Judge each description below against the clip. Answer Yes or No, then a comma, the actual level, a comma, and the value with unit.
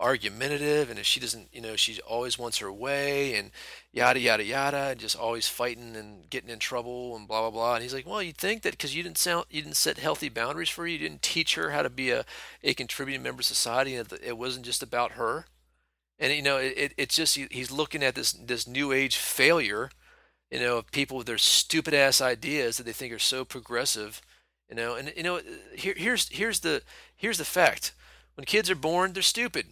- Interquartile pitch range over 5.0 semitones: No, average, 4.7 semitones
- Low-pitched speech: Yes, low, 130 Hz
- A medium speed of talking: No, fast, 230 wpm